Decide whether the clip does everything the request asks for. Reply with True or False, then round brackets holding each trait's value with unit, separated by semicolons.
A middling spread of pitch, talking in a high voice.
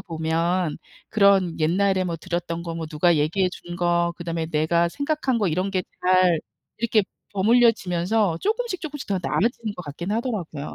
False (3.9 semitones; 180 Hz)